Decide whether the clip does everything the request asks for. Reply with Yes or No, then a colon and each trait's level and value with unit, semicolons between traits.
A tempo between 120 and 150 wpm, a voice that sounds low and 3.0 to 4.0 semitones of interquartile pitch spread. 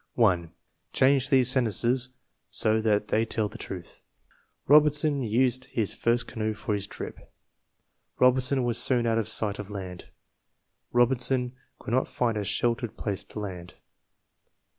Yes: average, 140 wpm; low, 115 Hz; average, 3.5 semitones